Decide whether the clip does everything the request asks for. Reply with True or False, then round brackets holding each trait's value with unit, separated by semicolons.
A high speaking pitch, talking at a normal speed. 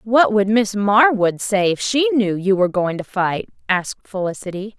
True (205 Hz; 190 wpm)